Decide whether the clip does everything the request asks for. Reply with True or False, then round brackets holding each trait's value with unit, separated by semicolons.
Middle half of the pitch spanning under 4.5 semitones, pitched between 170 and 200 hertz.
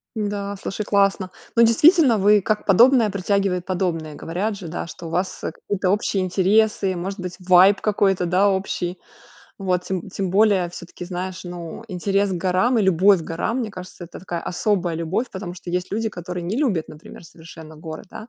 True (2.5 semitones; 190 Hz)